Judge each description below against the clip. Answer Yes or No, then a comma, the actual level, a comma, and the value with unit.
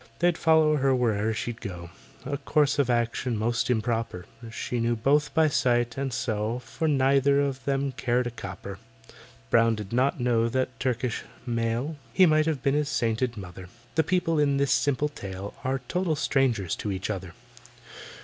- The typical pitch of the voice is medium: No, low, 125 Hz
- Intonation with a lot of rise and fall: No, average, 3.8 semitones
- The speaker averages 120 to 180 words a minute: Yes, average, 170 wpm